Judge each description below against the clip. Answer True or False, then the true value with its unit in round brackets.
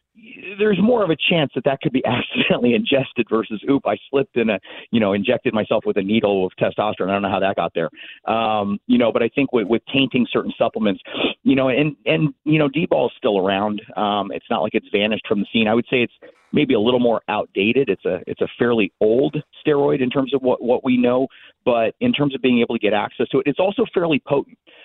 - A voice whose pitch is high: False (130 Hz)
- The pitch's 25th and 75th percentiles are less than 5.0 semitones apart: False (5.5 semitones)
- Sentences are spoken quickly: True (245 wpm)